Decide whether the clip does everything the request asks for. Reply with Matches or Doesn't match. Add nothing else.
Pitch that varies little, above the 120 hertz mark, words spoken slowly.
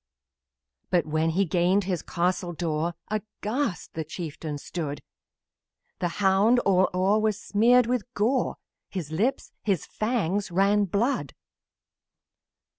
Doesn't match